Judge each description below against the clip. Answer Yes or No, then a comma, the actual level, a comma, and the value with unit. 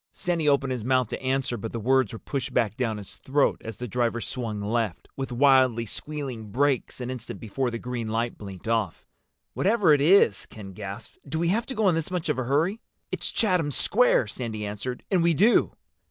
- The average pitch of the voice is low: Yes, low, 125 Hz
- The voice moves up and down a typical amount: Yes, average, 4.8 semitones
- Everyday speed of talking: No, fast, 210 wpm